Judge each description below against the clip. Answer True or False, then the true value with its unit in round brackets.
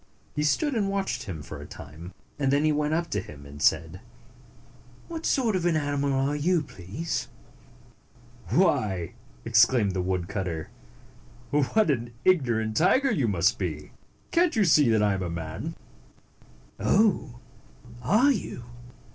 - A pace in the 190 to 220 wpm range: False (155 wpm)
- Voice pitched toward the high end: False (130 Hz)